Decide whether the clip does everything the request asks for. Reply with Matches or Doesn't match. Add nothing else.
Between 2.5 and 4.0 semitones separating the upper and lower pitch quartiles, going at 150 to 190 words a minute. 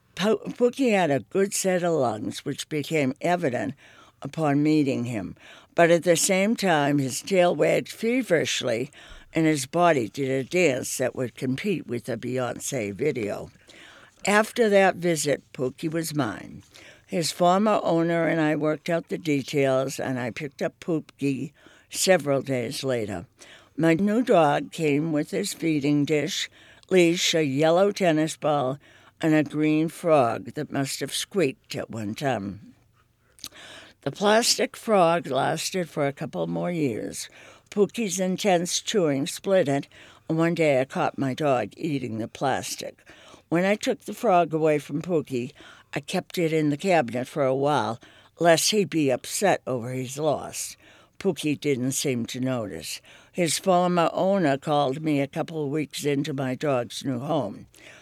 Doesn't match